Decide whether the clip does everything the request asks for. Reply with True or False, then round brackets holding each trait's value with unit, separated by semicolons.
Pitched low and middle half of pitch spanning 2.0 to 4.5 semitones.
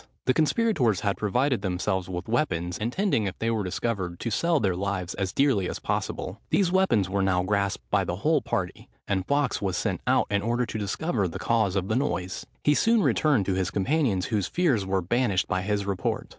False (100 Hz; 4.9 semitones)